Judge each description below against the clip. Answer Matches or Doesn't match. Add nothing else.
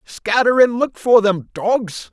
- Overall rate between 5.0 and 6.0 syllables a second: Doesn't match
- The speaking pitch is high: Matches